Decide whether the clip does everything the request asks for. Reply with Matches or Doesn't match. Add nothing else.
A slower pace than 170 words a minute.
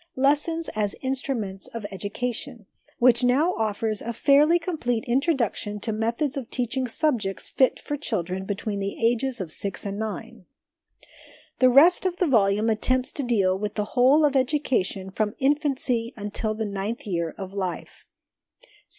Matches